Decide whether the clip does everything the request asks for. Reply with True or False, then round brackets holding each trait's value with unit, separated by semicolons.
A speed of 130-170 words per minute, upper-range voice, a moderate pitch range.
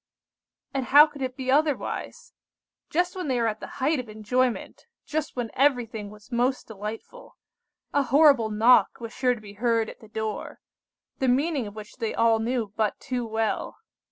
False (180 wpm; 245 Hz; 3.7 semitones)